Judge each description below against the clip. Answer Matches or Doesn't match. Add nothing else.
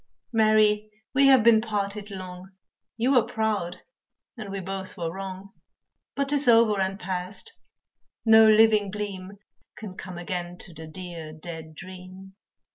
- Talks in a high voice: Matches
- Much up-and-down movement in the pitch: Doesn't match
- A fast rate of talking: Doesn't match